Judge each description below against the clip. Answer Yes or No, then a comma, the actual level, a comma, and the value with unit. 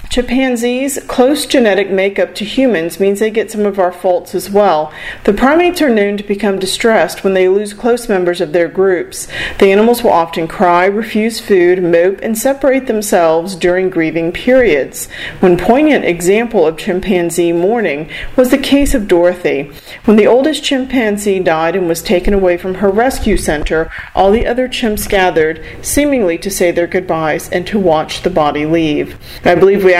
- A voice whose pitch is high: Yes, high, 195 Hz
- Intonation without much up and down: No, average, 4.6 semitones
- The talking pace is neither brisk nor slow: Yes, average, 175 wpm